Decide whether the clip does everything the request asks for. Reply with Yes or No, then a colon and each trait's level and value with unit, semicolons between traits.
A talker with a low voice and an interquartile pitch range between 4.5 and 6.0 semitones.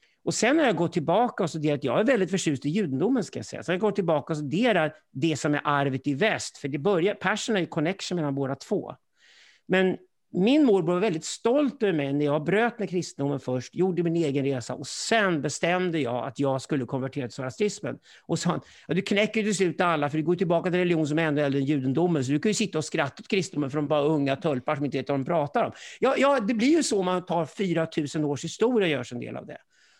No: medium, 165 Hz; average, 5.0 semitones